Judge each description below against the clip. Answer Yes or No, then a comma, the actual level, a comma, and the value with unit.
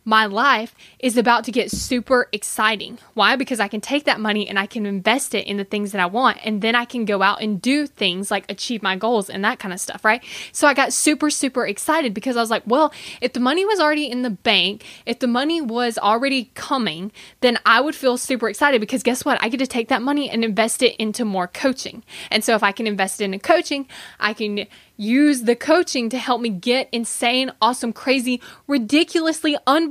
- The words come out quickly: Yes, fast, 230 wpm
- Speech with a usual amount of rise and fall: Yes, average, 3.7 semitones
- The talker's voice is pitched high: Yes, high, 240 Hz